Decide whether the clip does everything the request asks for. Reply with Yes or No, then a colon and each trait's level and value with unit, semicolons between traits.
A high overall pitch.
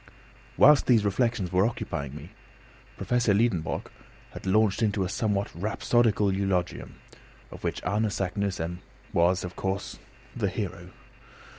No: low, 100 Hz